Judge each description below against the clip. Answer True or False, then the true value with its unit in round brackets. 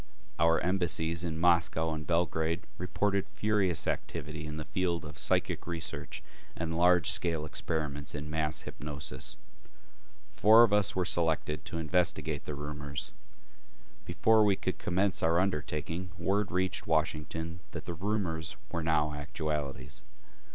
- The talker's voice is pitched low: True (80 Hz)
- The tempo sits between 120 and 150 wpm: True (135 wpm)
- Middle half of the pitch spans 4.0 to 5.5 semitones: False (2.9 semitones)